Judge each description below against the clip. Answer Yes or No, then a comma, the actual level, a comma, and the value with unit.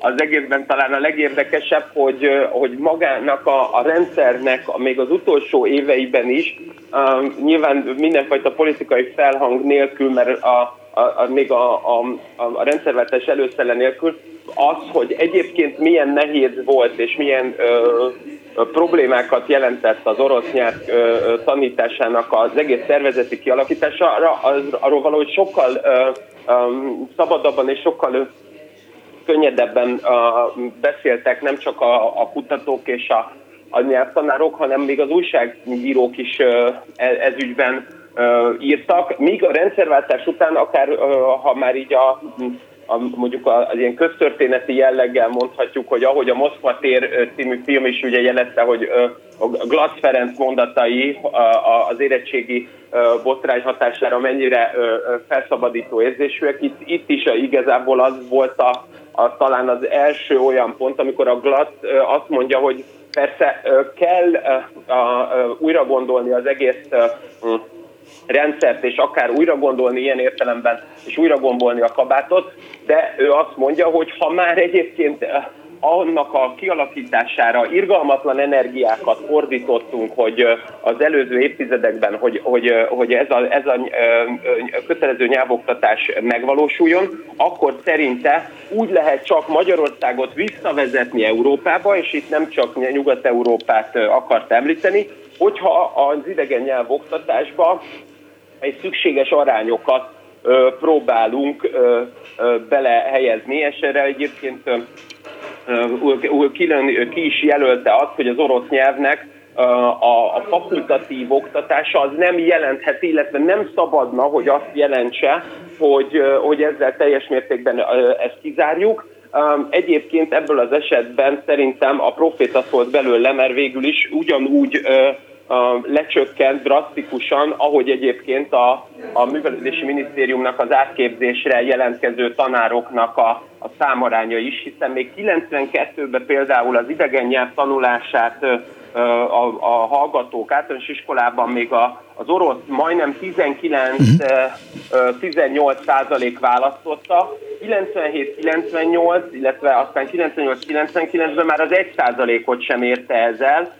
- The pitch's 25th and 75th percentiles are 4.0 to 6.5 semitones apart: Yes, average, 4.7 semitones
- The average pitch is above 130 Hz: Yes, medium, 140 Hz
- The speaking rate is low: No, average, 120 wpm